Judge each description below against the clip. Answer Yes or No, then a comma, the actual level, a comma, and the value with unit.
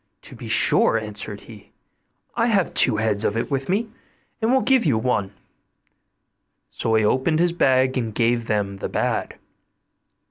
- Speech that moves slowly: No, average, 165 wpm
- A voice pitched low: Yes, low, 130 Hz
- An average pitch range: No, wide, 8.0 semitones